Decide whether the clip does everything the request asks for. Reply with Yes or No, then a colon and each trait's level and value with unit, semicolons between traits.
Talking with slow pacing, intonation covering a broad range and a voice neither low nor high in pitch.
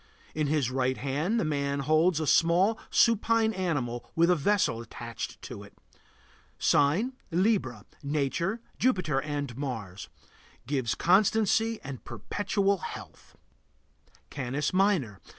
Yes: slow, 115 wpm; wide, 6.6 semitones; medium, 155 Hz